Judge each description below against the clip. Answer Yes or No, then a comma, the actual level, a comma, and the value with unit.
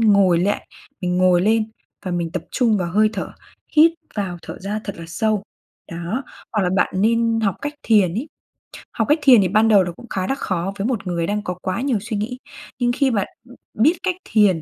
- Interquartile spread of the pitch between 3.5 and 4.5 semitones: Yes, average, 4.0 semitones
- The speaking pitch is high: Yes, high, 210 Hz